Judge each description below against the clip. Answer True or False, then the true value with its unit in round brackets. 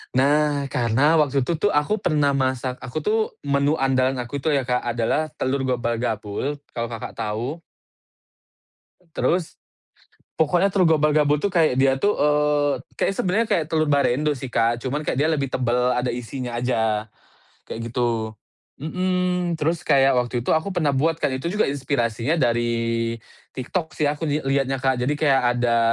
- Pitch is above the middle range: False (140 Hz)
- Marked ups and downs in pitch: False (3.9 semitones)